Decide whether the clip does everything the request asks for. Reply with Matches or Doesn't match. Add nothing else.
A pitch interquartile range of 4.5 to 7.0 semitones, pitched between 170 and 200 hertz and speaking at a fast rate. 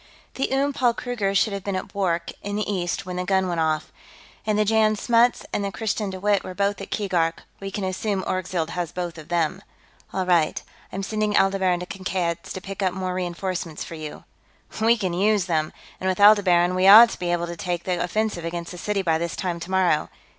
Doesn't match